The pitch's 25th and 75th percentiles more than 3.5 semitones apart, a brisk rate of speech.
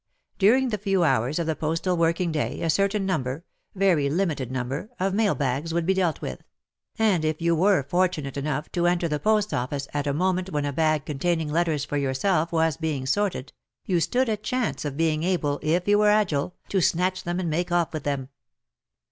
Yes: average, 4.3 semitones; fast, 210 wpm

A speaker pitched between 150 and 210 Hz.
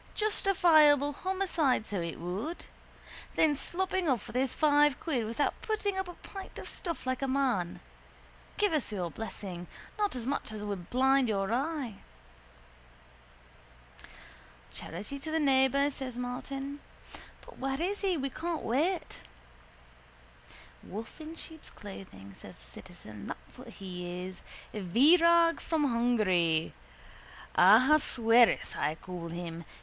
No: very high, 265 Hz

